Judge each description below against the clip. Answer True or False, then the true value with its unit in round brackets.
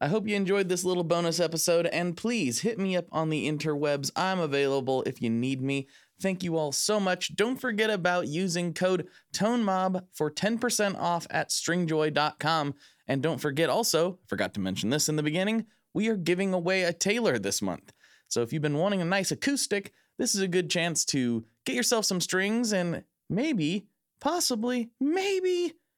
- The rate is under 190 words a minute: True (180 wpm)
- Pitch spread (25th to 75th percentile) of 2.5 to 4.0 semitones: False (5.1 semitones)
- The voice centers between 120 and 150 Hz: False (180 Hz)